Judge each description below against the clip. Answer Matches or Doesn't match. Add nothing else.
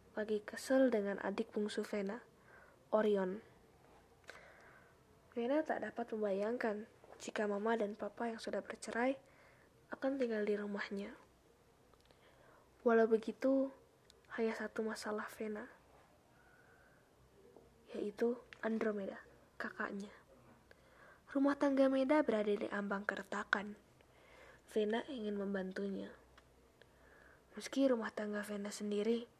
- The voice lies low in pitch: Doesn't match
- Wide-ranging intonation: Doesn't match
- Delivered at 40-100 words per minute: Matches